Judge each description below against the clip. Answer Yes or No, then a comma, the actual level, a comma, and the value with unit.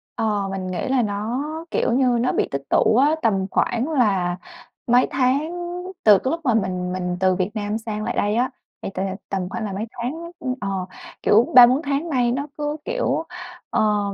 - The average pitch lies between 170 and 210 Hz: No, high, 225 Hz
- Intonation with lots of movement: No, average, 4.8 semitones